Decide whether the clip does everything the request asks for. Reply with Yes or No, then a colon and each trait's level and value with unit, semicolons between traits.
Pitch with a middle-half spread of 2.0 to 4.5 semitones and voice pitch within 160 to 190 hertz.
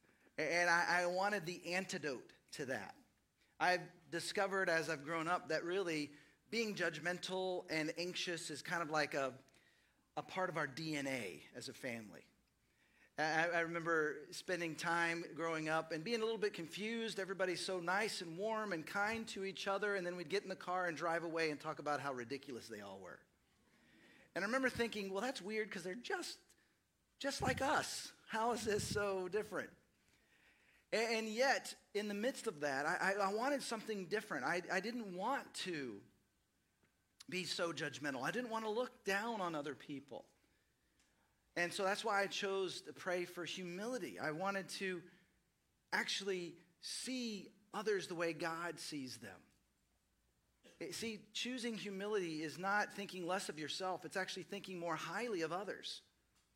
Yes: average, 4.0 semitones; medium, 185 Hz